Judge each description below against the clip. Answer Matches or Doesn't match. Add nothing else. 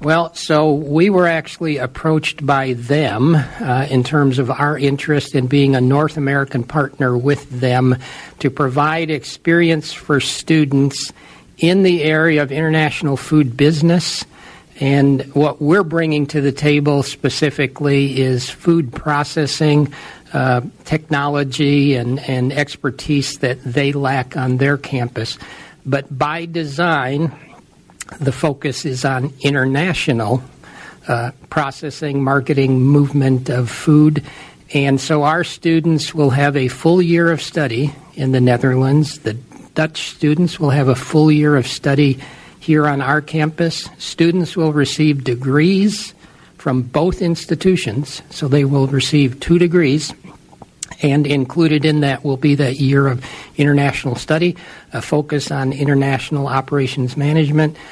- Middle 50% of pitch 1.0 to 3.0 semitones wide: Matches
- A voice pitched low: Doesn't match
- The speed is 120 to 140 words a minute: Matches